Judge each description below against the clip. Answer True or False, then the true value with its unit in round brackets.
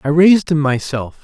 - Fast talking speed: False (195 wpm)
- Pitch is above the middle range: False (150 Hz)